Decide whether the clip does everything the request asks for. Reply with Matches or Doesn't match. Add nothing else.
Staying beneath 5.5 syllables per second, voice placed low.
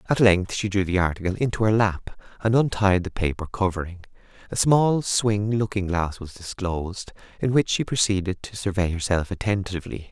Matches